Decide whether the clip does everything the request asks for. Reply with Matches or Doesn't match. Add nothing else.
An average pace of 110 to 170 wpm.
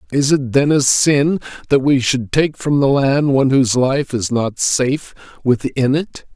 Doesn't match